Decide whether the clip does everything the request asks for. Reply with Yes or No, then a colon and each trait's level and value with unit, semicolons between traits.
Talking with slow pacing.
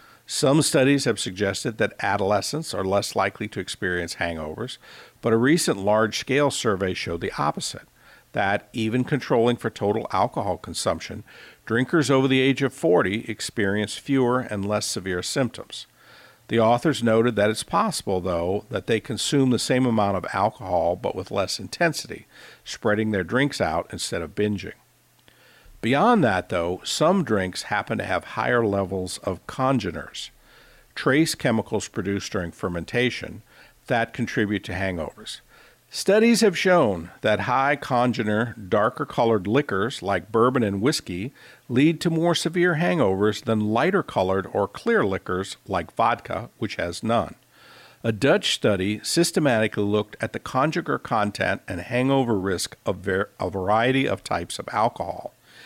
No: average, 145 wpm